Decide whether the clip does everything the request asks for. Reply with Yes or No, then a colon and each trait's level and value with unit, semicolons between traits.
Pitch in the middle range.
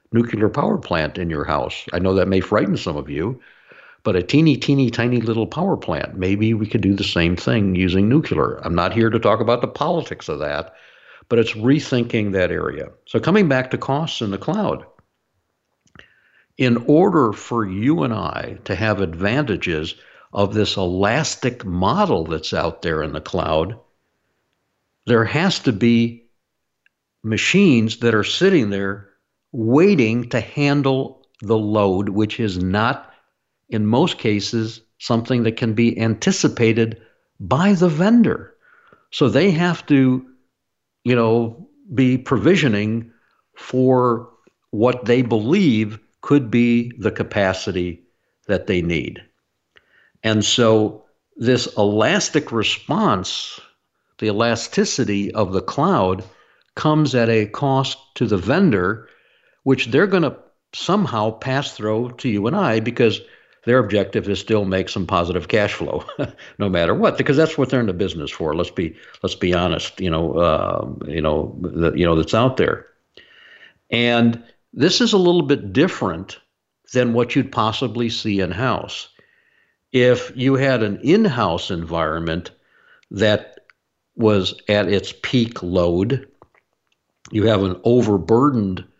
No: low, 115 Hz